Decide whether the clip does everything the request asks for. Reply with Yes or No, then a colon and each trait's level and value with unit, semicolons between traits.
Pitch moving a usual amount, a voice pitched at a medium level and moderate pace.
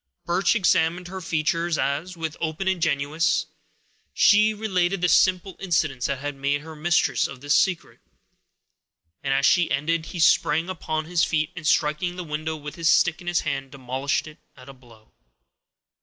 Yes: average, 3.5 semitones; medium, 160 Hz; average, 170 wpm